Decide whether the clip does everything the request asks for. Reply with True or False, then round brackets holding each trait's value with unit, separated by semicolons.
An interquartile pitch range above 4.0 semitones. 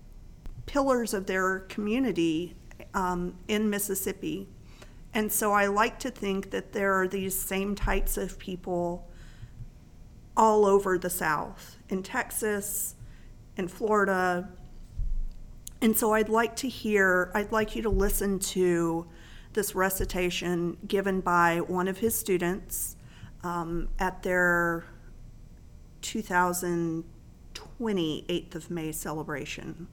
False (3.3 semitones)